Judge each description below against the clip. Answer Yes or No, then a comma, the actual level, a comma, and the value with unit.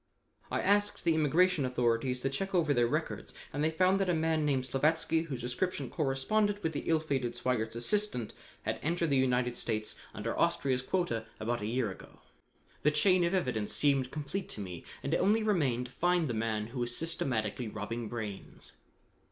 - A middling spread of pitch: No, wide, 5.8 semitones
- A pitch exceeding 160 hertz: No, low, 135 Hz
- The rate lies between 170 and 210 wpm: Yes, average, 185 wpm